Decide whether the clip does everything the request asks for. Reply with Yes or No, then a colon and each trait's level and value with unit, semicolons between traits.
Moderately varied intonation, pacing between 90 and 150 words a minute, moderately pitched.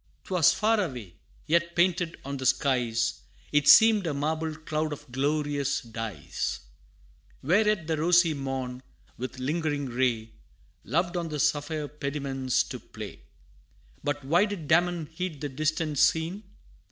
Yes: average, 4.1 semitones; average, 140 wpm; medium, 150 Hz